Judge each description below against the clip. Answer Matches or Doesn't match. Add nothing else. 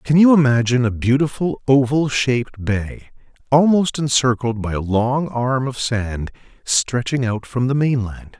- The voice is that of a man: Matches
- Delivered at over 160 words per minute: Doesn't match